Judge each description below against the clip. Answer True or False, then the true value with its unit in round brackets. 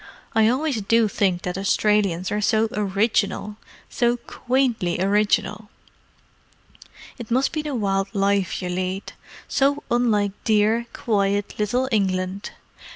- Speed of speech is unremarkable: False (115 wpm)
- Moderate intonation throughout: True (3.0 semitones)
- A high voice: True (210 Hz)